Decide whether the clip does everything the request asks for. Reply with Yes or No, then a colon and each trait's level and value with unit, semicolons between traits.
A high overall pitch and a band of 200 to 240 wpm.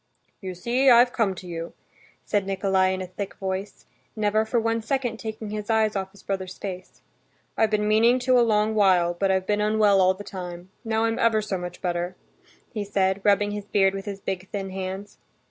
Yes: high, 200 Hz; fast, 205 wpm